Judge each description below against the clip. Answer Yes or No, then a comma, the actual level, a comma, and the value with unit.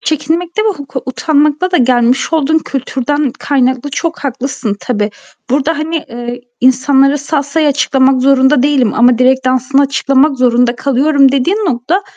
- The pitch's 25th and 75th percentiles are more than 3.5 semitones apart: No, average, 2.8 semitones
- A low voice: No, very high, 275 Hz